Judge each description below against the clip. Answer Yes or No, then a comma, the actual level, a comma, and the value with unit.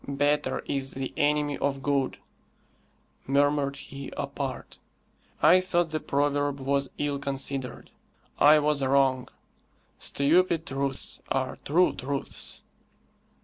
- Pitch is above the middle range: No, medium, 140 Hz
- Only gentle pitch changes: Yes, narrow, 1.4 semitones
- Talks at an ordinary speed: No, slow, 105 wpm